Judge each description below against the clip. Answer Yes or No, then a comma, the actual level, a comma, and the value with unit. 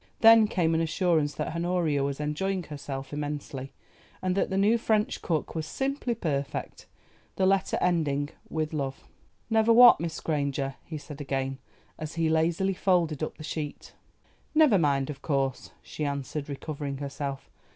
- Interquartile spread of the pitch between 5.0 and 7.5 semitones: No, average, 4.5 semitones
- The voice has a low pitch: No, medium, 155 Hz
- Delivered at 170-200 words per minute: No, average, 155 wpm